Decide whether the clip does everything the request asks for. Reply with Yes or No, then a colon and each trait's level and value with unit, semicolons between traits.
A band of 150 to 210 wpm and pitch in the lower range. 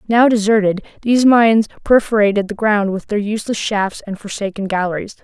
No: average, 160 wpm; high, 210 Hz